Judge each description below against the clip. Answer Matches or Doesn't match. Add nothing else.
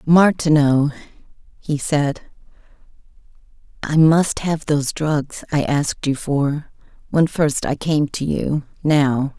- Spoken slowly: Matches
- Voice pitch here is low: Doesn't match